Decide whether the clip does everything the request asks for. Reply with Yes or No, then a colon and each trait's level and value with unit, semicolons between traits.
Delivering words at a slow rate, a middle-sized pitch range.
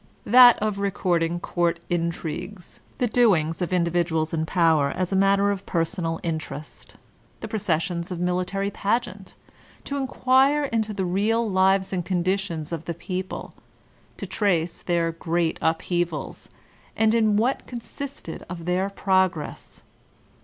Yes: slow, 130 wpm; average, 3.3 semitones